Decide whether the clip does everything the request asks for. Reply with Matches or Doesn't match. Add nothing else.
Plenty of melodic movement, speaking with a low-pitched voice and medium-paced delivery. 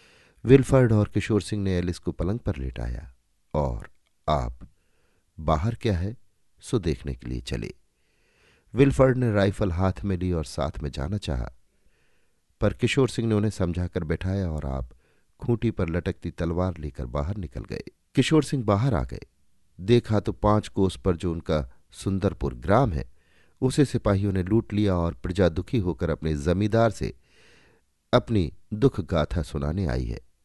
Doesn't match